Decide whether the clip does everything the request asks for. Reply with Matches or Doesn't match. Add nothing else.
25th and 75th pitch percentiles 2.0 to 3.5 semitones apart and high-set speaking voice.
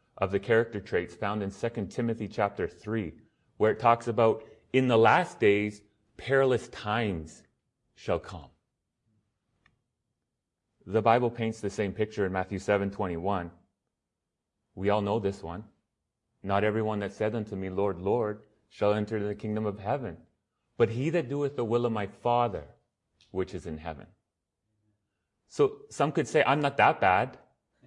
Doesn't match